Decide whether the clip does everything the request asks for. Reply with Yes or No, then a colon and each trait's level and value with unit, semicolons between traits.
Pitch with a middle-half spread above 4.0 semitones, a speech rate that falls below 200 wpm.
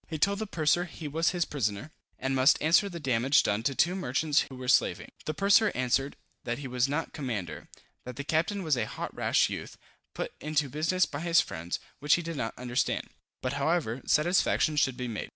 No: average, 4.7 semitones; fast, 205 wpm